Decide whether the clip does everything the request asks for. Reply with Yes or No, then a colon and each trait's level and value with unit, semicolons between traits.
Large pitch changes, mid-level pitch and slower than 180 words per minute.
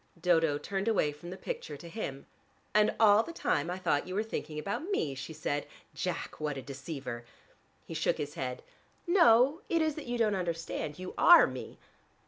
No: wide, 7.2 semitones; medium, 175 Hz; average, 190 wpm